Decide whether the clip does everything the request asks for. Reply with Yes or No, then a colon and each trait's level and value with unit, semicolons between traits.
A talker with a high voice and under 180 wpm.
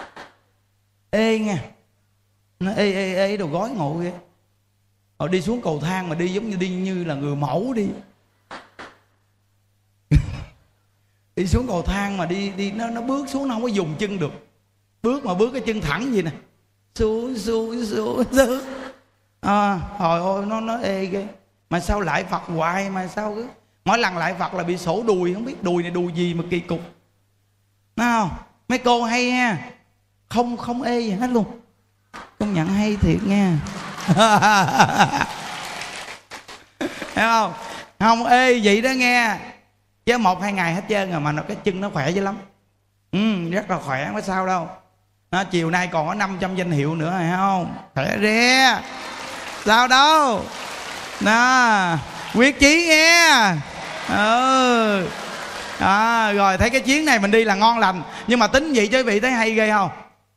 Yes: high, 195 Hz; average, 170 wpm